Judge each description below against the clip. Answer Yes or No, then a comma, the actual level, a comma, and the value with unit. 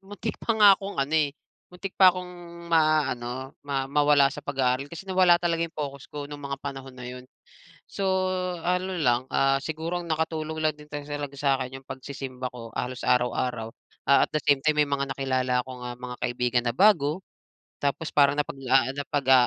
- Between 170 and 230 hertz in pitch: No, medium, 140 Hz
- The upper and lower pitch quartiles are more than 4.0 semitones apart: No, average, 3.5 semitones